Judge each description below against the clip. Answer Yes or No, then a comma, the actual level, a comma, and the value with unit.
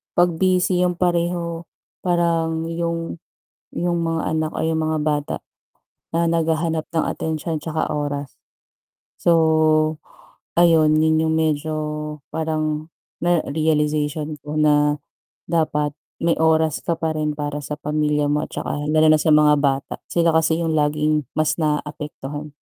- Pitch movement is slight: Yes, narrow, 1.6 semitones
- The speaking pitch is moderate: Yes, medium, 155 Hz